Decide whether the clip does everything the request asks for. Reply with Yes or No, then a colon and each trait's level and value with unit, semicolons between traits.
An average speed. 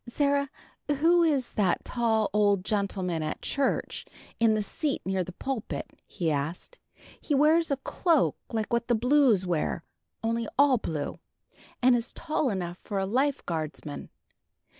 Yes: average, 150 wpm